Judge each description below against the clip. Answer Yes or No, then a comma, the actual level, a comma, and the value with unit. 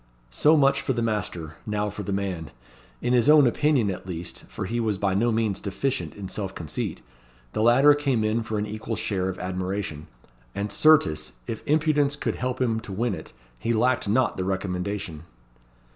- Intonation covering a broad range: No, average, 4.6 semitones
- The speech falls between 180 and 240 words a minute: Yes, average, 190 wpm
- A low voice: Yes, low, 105 Hz